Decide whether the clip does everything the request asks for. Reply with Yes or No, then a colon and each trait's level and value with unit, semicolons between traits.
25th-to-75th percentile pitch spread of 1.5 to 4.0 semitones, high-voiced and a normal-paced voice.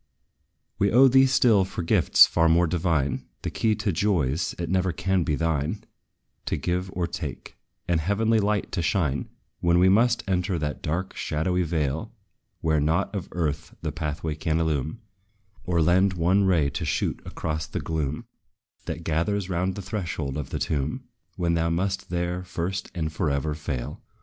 No: average, 3.4 semitones; very low, 85 Hz; average, 170 wpm